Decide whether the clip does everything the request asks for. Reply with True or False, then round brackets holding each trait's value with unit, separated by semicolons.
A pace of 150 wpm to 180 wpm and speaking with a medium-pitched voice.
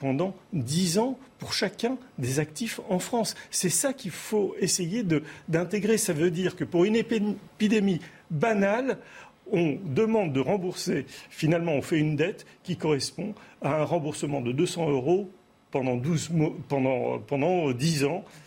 True (155 wpm; 175 Hz)